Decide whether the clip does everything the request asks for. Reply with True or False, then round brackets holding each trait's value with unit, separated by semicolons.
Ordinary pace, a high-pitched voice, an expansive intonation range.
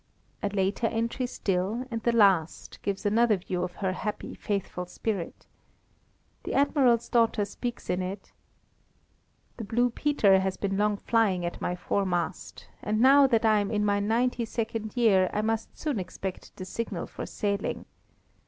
False (160 wpm; 210 Hz; 3.3 semitones)